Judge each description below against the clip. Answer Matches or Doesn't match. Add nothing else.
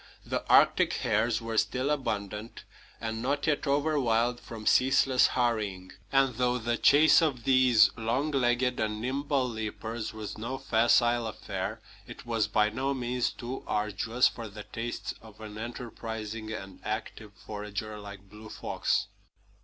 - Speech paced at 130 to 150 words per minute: Matches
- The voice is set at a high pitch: Doesn't match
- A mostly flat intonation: Doesn't match